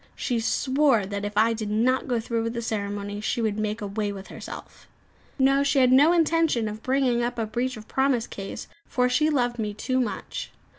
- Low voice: No, high, 235 Hz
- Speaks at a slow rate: No, fast, 205 wpm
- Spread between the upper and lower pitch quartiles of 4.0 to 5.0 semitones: No, average, 3.5 semitones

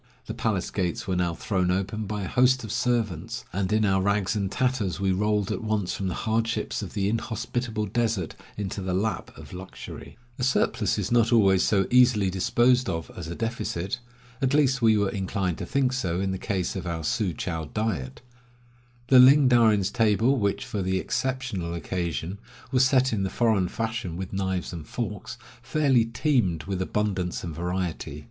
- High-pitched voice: No, low, 100 Hz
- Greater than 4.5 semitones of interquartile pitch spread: No, average, 4.2 semitones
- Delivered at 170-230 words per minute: Yes, average, 190 wpm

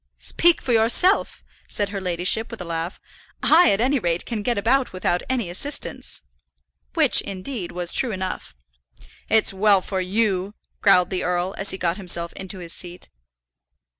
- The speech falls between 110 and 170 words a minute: Yes, average, 165 wpm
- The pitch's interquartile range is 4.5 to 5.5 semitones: No, average, 4.1 semitones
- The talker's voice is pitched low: No, high, 195 Hz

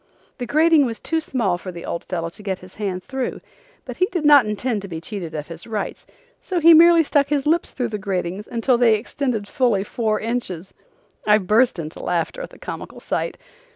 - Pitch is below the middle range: No, high, 220 Hz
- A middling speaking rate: No, fast, 210 wpm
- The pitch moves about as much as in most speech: No, wide, 6.9 semitones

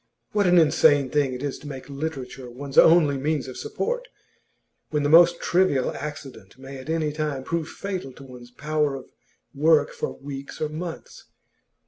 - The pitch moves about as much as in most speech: Yes, average, 3.0 semitones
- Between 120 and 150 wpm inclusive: No, average, 170 wpm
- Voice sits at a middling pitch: Yes, medium, 145 Hz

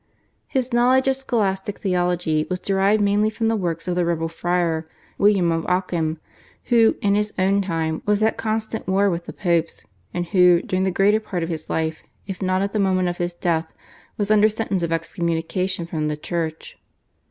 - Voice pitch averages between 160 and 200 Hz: Yes, medium, 185 Hz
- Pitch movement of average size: Yes, average, 3.4 semitones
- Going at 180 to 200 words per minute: Yes, average, 190 wpm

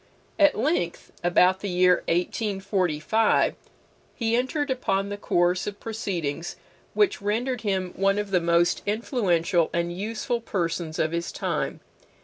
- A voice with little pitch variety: No, average, 4.4 semitones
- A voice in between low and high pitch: No, high, 195 Hz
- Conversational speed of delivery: No, slow, 130 wpm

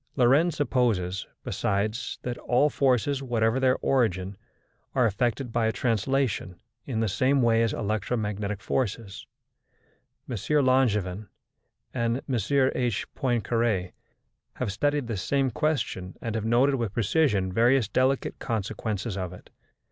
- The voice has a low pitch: Yes, low, 115 Hz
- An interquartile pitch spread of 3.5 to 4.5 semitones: Yes, average, 4.0 semitones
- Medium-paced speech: No, slow, 125 wpm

